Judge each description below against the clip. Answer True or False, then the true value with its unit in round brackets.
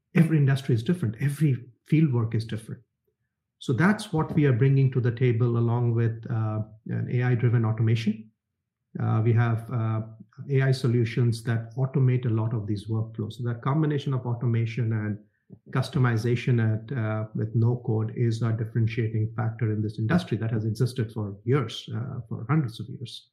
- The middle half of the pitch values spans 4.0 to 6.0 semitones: False (2.5 semitones)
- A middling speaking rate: True (170 wpm)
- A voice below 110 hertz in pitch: False (120 Hz)